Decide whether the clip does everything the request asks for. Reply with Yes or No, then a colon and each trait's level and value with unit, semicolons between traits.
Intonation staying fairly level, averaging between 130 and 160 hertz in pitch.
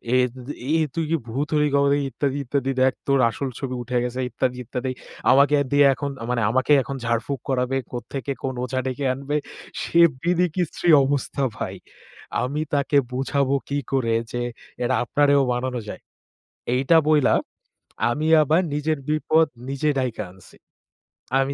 Yes: narrow, 2.3 semitones; low, 135 Hz